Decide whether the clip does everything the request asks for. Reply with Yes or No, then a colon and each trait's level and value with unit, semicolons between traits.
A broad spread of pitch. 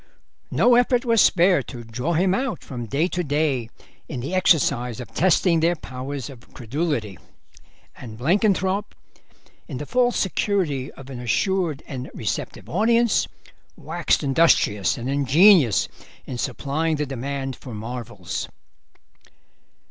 Yes: wide, 6.4 semitones